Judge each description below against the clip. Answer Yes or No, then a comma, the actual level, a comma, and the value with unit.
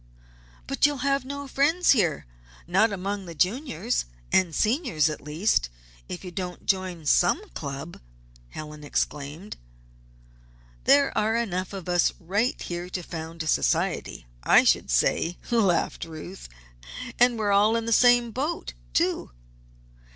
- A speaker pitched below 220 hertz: Yes, high, 190 Hz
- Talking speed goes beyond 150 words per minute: No, slow, 135 wpm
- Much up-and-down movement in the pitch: Yes, wide, 6.2 semitones